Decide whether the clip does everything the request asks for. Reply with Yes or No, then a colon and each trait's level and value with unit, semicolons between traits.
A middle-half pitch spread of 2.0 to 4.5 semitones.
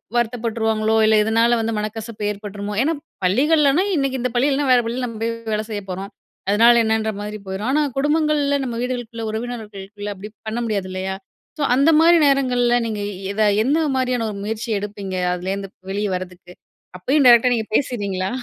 Yes: average, 3.4 semitones